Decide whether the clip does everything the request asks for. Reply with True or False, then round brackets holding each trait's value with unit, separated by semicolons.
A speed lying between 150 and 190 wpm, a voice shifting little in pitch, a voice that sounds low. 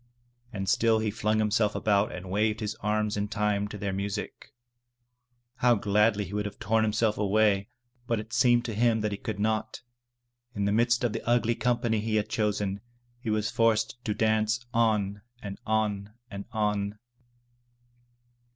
True (170 wpm; 1.6 semitones; 105 Hz)